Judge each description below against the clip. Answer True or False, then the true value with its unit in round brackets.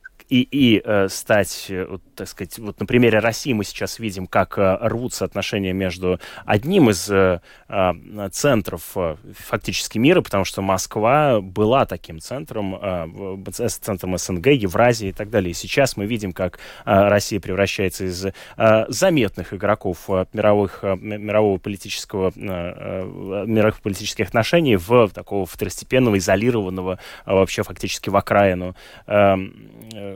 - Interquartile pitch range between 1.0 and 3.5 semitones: True (2.7 semitones)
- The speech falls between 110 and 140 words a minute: False (150 wpm)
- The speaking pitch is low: True (100 Hz)